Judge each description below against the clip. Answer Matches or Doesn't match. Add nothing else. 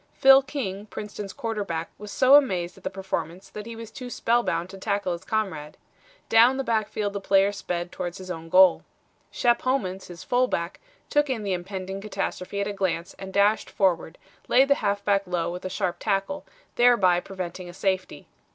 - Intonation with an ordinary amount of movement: Matches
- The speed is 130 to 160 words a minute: Doesn't match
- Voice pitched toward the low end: Doesn't match